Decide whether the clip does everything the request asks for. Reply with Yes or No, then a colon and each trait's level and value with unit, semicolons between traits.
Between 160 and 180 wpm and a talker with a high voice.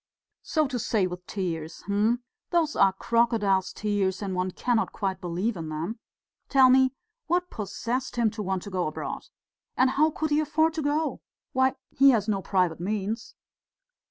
Yes: average, 170 wpm; high, 215 Hz